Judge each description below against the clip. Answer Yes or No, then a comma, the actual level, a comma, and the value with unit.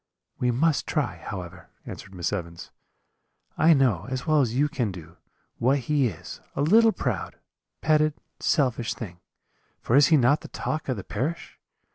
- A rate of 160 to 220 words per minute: Yes, average, 165 wpm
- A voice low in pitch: Yes, low, 125 Hz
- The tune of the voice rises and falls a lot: Yes, wide, 7.3 semitones